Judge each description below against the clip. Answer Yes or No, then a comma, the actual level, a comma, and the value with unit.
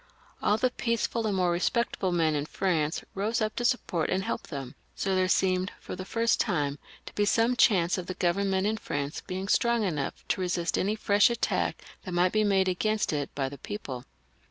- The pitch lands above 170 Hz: Yes, high, 190 Hz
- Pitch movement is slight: No, average, 3.8 semitones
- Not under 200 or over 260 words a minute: Yes, fast, 205 wpm